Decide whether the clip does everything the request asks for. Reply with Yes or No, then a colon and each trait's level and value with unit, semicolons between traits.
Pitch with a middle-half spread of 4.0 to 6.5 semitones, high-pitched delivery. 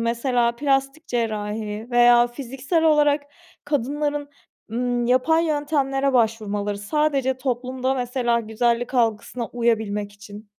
No: average, 3.2 semitones; high, 245 Hz